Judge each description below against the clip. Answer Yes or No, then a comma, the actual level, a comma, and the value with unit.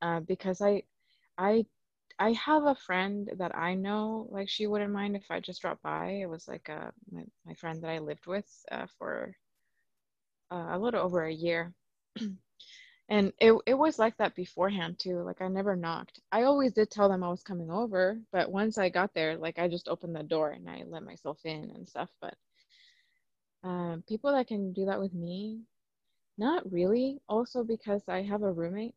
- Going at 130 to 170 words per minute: No, average, 195 wpm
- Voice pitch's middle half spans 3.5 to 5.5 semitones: Yes, average, 4.0 semitones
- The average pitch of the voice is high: Yes, high, 195 Hz